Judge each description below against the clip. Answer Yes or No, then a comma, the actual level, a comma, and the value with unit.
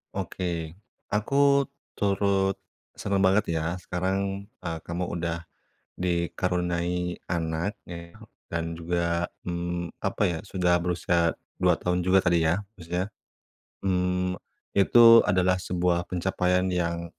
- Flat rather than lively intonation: Yes, narrow, 1.5 semitones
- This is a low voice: Yes, very low, 90 Hz